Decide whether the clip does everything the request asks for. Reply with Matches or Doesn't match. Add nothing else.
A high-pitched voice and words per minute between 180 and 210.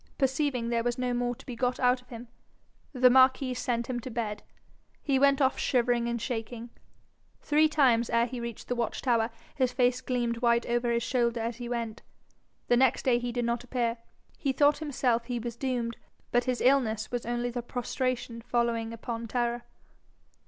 Matches